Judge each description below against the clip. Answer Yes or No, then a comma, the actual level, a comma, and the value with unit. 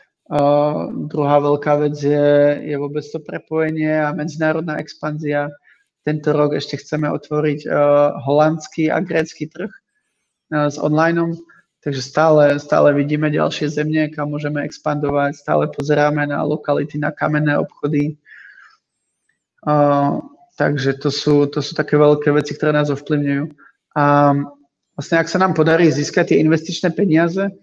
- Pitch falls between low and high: Yes, medium, 150 Hz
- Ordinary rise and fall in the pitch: No, narrow, 1.3 semitones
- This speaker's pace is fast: No, average, 135 wpm